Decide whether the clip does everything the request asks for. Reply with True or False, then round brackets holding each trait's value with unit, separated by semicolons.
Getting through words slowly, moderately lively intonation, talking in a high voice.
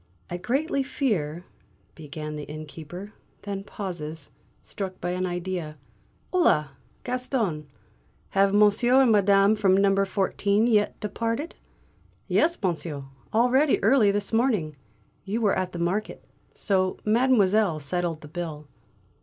True (125 wpm; 4.7 semitones; 195 Hz)